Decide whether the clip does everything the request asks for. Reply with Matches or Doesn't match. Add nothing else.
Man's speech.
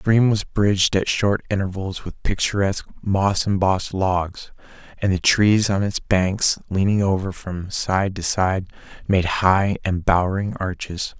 Matches